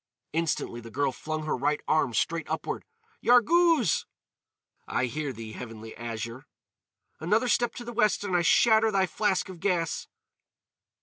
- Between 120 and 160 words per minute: Yes, average, 145 wpm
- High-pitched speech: No, medium, 165 Hz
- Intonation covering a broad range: Yes, wide, 8.9 semitones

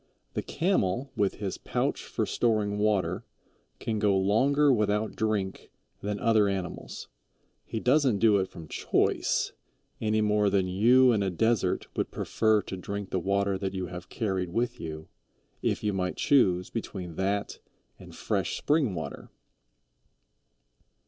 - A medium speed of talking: Yes, average, 145 wpm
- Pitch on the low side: Yes, low, 105 Hz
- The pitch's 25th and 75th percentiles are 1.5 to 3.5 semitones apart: Yes, average, 2.9 semitones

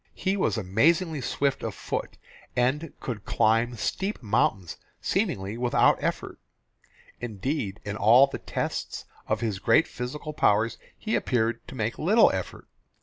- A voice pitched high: No, low, 120 Hz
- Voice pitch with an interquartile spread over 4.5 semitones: Yes, wide, 5.5 semitones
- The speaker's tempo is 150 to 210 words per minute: No, average, 140 wpm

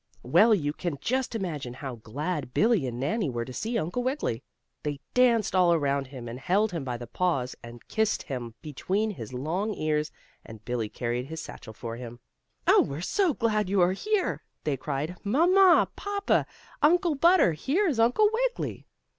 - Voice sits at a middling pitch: Yes, medium, 170 Hz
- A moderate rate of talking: Yes, average, 180 wpm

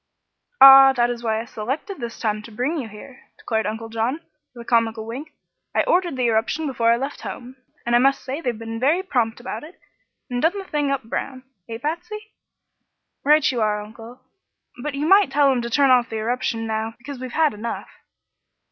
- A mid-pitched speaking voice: No, high, 245 Hz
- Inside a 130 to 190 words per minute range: No, fast, 205 wpm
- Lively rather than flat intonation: No, average, 3.9 semitones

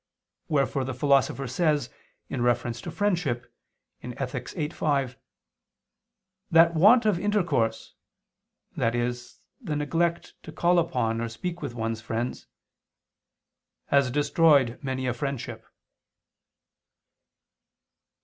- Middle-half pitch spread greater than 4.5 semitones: Yes, wide, 5.4 semitones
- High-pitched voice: No, low, 135 Hz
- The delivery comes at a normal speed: No, slow, 100 wpm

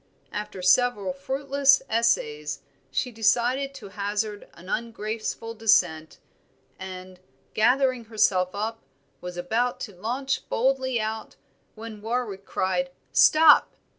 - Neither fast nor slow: No, slow, 105 wpm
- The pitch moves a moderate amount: Yes, average, 4.3 semitones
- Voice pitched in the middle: No, high, 225 Hz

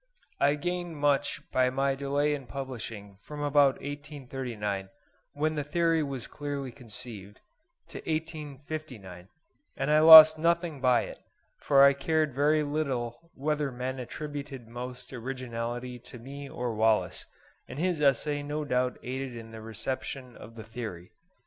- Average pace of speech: Yes, average, 145 wpm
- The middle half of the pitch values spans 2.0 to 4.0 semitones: Yes, average, 3.5 semitones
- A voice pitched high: No, low, 135 Hz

